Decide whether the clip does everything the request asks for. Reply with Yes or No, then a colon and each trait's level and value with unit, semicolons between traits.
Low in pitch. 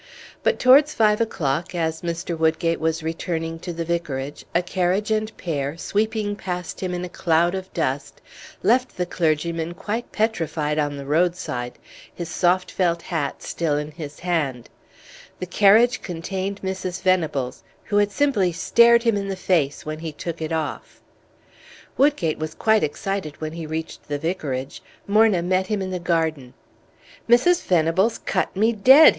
No: medium, 175 Hz